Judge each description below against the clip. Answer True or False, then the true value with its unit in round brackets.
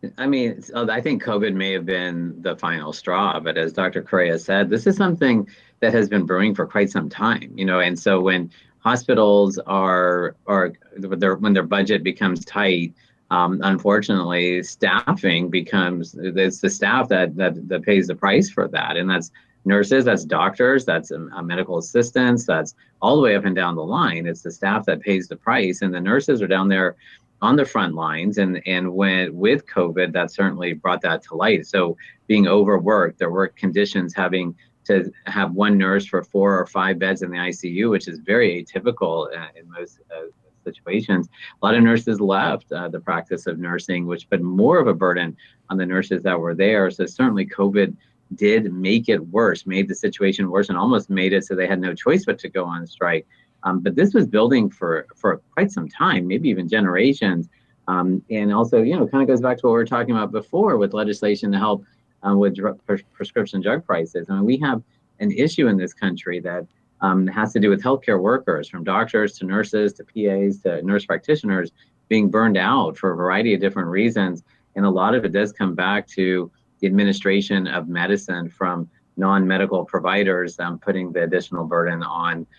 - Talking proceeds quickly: False (195 wpm)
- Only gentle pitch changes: True (2.3 semitones)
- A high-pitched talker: False (95 Hz)